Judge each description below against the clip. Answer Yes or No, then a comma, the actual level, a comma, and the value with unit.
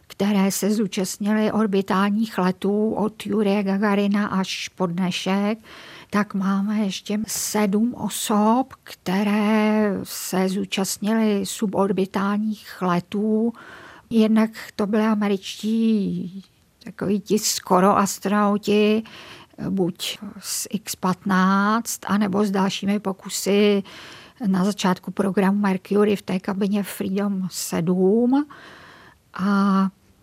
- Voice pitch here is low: No, high, 200 Hz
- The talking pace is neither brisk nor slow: No, slow, 90 wpm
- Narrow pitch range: Yes, narrow, 1.7 semitones